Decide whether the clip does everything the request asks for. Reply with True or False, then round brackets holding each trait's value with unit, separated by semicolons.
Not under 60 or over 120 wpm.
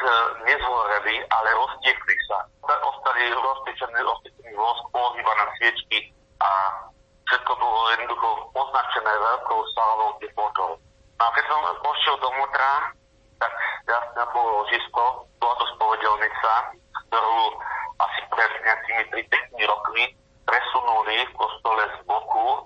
True (110 wpm)